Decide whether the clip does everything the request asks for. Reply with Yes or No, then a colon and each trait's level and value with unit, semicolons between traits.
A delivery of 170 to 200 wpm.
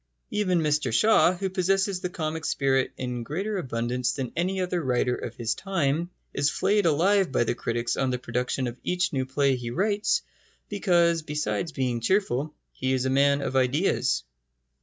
Yes: average, 175 wpm